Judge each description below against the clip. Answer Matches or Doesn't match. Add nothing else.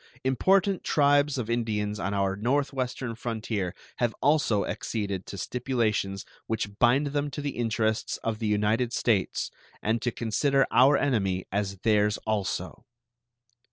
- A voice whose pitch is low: Matches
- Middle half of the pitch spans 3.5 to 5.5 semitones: Matches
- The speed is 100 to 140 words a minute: Matches